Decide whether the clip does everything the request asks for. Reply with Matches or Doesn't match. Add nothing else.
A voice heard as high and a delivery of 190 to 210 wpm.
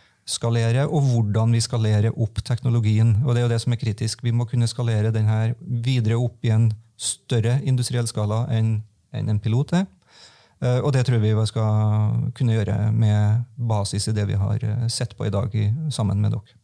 Doesn't match